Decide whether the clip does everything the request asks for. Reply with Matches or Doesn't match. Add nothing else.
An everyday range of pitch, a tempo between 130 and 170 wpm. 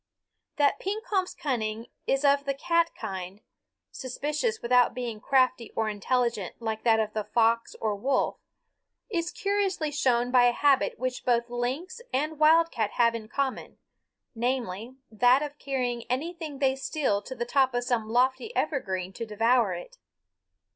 Matches